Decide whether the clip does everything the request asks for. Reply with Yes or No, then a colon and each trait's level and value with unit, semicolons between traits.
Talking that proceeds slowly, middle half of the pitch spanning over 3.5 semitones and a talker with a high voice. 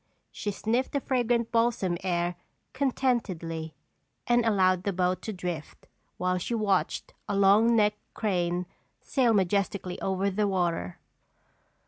Yes: slow, 125 wpm; average, 4.1 semitones; high, 195 Hz